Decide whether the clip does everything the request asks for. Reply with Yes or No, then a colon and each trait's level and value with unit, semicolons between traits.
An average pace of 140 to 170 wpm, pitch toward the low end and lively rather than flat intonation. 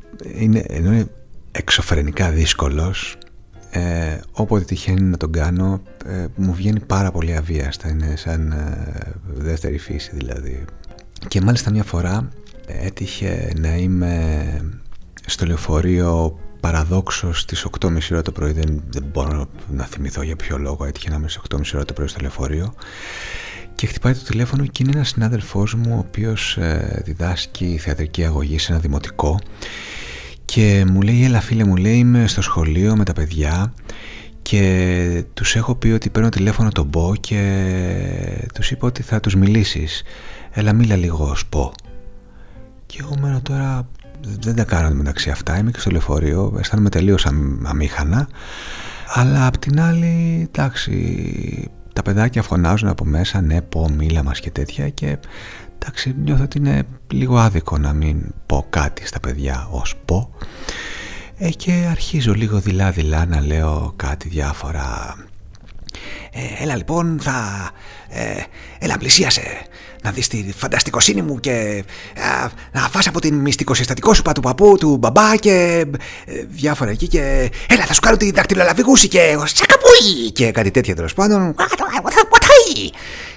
Yes: average, 145 wpm; very low, 95 Hz; wide, 6.6 semitones